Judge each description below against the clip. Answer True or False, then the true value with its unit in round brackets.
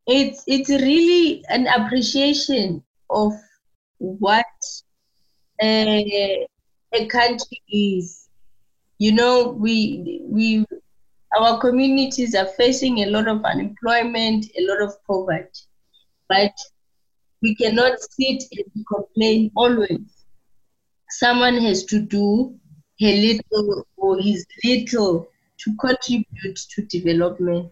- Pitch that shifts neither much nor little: True (3.5 semitones)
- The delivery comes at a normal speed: False (100 wpm)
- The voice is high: True (220 Hz)